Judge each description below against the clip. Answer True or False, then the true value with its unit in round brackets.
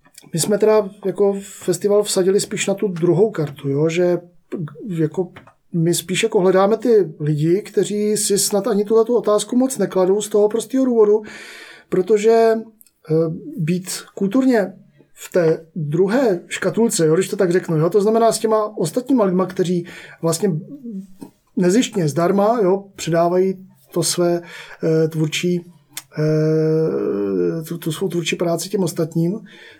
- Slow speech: False (135 wpm)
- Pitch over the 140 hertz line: True (185 Hz)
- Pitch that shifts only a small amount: False (3.8 semitones)